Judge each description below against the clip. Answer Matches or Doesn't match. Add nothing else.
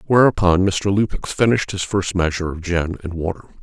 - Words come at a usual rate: Matches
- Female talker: Doesn't match